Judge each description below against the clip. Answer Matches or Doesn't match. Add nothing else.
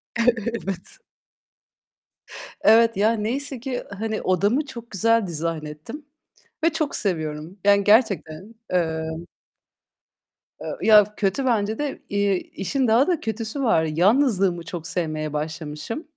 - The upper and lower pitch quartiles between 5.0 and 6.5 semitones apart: Matches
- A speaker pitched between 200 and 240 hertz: Matches